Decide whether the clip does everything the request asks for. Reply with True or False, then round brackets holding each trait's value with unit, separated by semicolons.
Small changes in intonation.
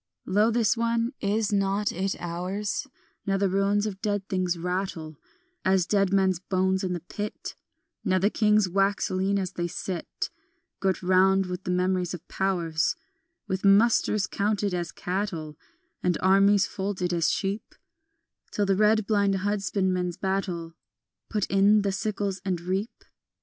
True (2.0 semitones)